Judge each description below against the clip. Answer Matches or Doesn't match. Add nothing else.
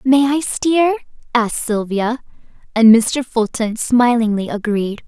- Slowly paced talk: Matches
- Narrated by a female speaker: Matches